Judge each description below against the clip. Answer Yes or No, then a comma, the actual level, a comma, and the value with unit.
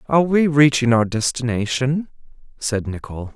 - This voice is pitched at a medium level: No, low, 130 Hz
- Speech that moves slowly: Yes, slow, 125 wpm